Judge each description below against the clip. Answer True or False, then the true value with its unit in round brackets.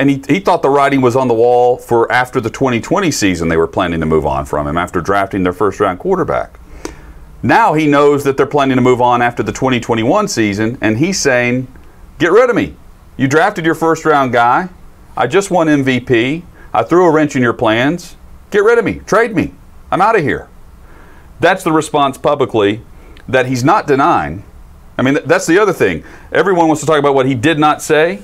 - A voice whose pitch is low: True (130 Hz)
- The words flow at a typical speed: False (215 wpm)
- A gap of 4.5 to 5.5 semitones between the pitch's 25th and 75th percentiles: True (5.1 semitones)